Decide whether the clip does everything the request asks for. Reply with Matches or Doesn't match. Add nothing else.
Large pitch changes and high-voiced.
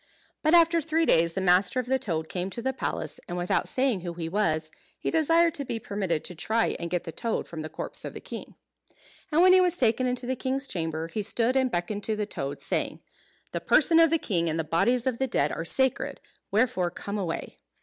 Matches